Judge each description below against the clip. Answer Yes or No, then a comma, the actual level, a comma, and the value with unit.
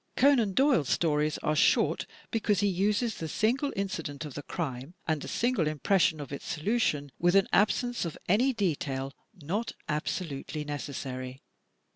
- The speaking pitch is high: No, medium, 165 Hz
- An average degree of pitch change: No, wide, 6.3 semitones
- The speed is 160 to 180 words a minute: No, average, 150 wpm